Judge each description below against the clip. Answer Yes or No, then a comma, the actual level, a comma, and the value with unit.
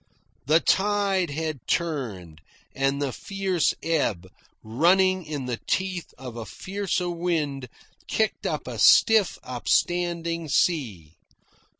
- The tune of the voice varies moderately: No, wide, 6.2 semitones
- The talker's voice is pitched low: No, medium, 165 Hz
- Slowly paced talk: Yes, slow, 110 wpm